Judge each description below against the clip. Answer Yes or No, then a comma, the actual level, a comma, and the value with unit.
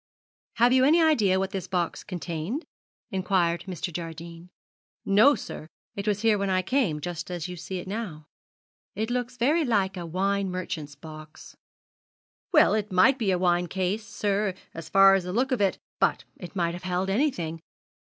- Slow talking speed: No, average, 185 wpm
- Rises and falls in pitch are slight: No, average, 3.6 semitones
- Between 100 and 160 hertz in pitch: No, high, 190 Hz